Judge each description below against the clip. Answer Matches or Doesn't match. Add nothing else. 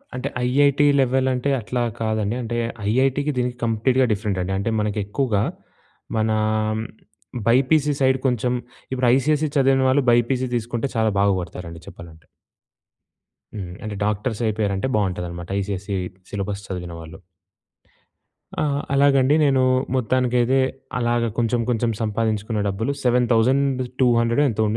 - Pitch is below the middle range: Matches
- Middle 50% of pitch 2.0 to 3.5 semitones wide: Doesn't match